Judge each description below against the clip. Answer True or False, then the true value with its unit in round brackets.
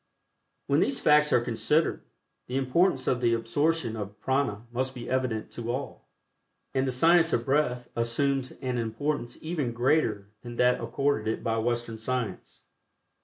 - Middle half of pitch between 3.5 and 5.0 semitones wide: False (3.1 semitones)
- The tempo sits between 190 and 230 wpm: False (155 wpm)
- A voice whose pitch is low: True (125 Hz)